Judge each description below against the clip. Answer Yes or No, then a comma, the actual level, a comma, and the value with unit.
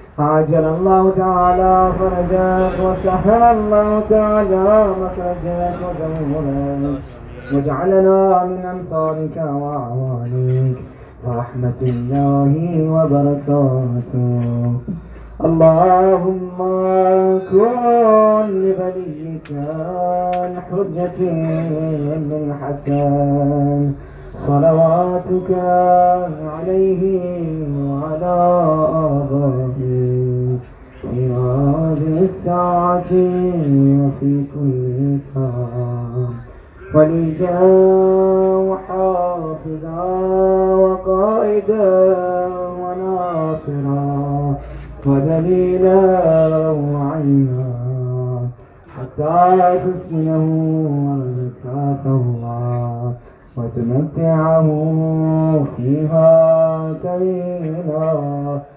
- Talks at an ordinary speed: No, slow, 40 wpm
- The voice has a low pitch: No, medium, 160 Hz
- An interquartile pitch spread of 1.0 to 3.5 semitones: No, average, 4.5 semitones